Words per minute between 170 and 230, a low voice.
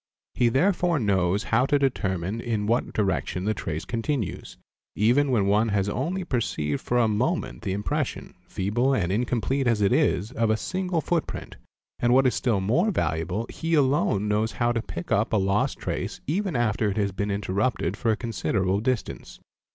Yes: average, 190 wpm; low, 110 Hz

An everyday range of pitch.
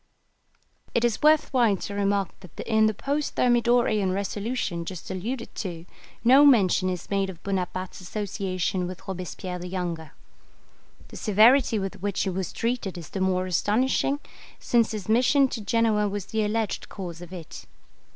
Yes: average, 3.9 semitones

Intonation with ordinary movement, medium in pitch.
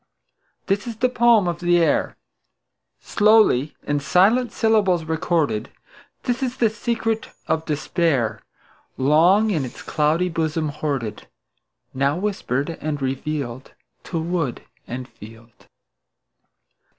No: wide, 6.9 semitones; medium, 160 Hz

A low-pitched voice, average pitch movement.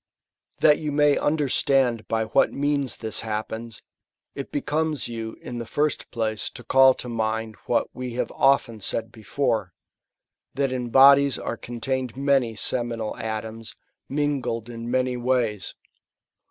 Yes: low, 120 Hz; average, 3.5 semitones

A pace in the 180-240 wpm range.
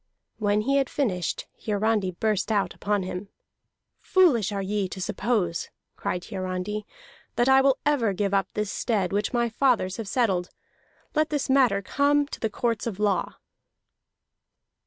No: average, 155 wpm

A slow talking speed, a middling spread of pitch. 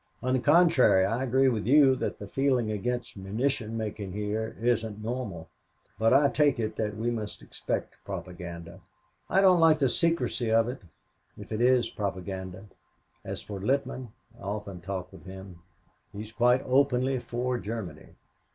No: average, 160 wpm; average, 4.4 semitones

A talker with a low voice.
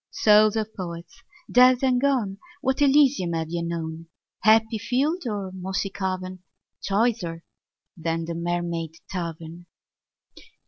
No: high, 190 Hz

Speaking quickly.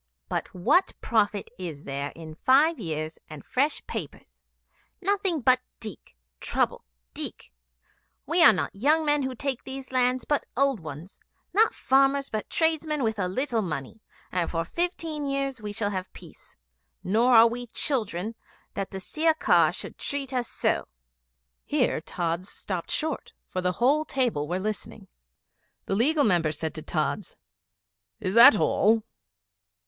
No: average, 150 wpm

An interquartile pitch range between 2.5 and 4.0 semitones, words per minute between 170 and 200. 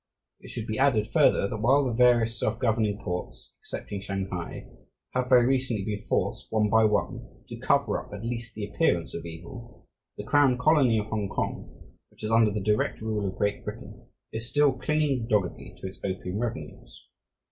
Yes: average, 3.4 semitones; average, 180 wpm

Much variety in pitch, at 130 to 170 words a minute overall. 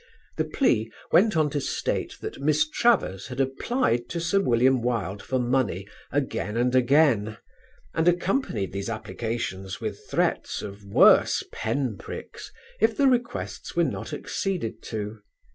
Yes: wide, 6.7 semitones; average, 145 wpm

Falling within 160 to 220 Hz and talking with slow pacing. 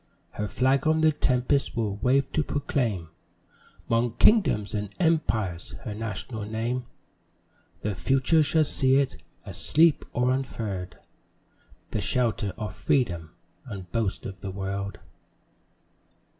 No: low, 115 Hz; slow, 120 wpm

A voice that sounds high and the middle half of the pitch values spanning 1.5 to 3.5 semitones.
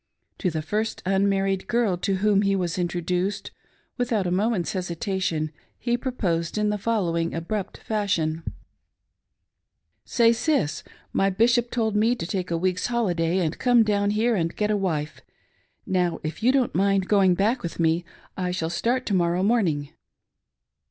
No: high, 195 Hz; average, 4.1 semitones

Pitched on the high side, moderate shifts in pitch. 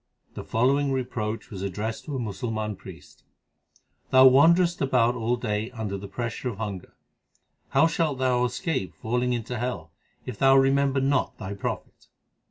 No: low, 125 Hz; average, 3.8 semitones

